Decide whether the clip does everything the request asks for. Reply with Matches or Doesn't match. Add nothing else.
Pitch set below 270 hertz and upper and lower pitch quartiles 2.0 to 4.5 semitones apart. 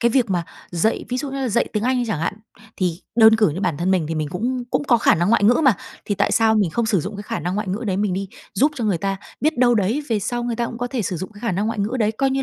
Matches